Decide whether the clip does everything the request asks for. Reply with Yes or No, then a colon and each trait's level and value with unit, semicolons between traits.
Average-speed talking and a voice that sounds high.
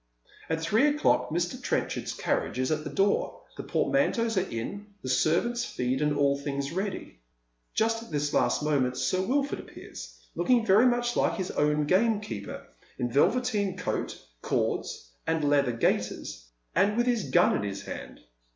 No: average, 160 wpm; medium, 175 Hz